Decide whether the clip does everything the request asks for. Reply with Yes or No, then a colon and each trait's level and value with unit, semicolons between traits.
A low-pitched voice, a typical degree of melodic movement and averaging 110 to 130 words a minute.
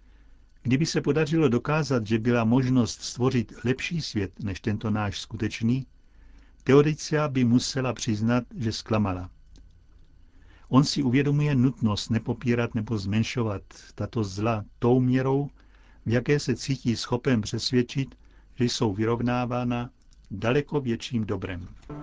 Yes: low, 120 Hz; average, 3.4 semitones; slow, 115 wpm